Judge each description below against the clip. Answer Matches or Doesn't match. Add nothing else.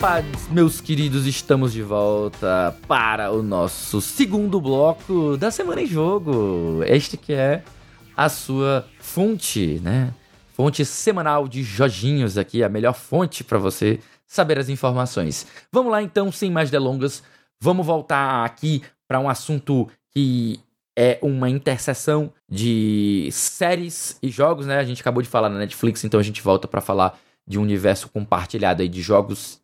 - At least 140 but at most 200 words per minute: Matches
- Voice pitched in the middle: Doesn't match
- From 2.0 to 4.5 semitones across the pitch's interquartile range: Doesn't match